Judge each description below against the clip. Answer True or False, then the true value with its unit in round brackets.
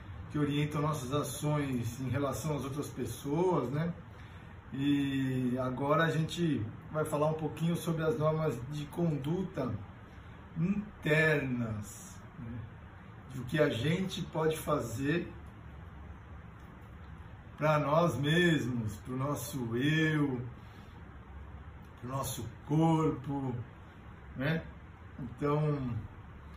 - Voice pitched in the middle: False (130 Hz)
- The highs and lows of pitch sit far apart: True (6.7 semitones)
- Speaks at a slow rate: True (100 wpm)